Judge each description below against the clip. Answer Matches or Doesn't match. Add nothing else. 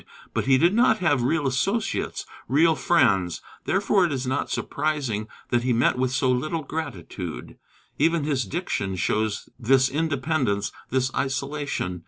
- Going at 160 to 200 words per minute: Doesn't match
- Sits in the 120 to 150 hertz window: Matches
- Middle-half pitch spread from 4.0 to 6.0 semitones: Matches